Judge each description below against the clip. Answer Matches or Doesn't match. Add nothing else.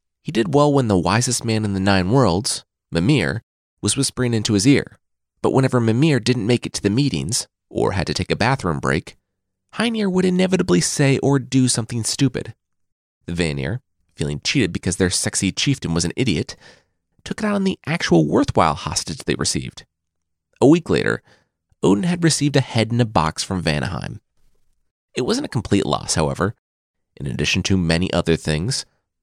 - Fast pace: Doesn't match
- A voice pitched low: Matches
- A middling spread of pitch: Doesn't match